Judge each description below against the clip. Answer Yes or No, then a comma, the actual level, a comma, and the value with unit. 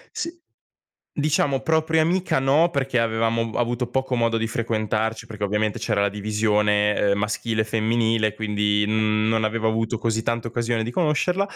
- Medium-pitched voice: No, low, 115 Hz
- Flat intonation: Yes, narrow, 2.2 semitones